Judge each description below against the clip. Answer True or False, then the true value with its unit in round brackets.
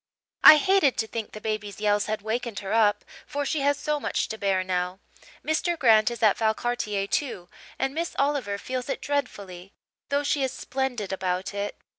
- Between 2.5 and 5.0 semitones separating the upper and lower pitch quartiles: False (5.6 semitones)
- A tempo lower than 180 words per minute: False (185 wpm)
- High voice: True (220 Hz)